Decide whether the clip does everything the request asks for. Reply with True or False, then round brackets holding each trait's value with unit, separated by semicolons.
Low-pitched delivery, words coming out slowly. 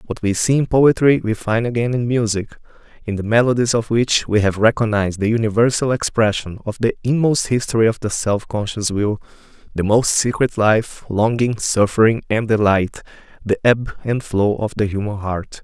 False (110 Hz; 175 wpm)